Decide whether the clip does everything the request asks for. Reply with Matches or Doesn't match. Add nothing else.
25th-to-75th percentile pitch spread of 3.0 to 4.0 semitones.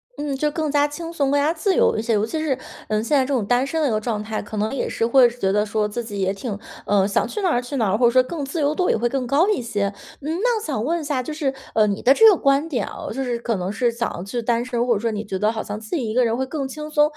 Doesn't match